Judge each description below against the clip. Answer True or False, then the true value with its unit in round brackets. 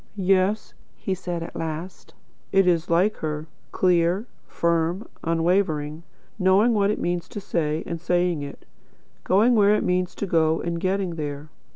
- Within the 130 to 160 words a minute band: True (155 wpm)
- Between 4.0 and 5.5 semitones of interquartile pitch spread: False (2.9 semitones)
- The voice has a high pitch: False (175 Hz)